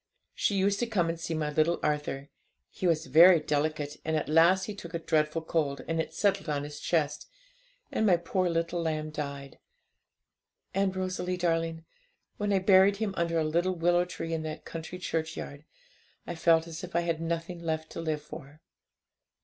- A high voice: No, medium, 165 Hz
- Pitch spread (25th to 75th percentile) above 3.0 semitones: No, narrow, 2.5 semitones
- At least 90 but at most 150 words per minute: No, average, 185 wpm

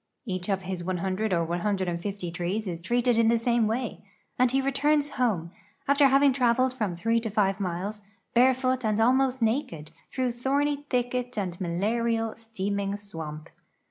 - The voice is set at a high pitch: Yes, high, 225 Hz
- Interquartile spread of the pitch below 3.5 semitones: No, average, 5.1 semitones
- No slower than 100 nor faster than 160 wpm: Yes, average, 155 wpm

